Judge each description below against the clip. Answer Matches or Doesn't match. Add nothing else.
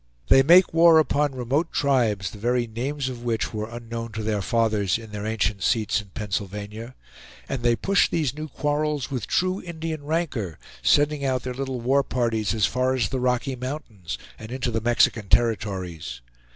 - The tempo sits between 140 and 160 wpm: Doesn't match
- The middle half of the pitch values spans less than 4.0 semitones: Doesn't match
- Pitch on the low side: Matches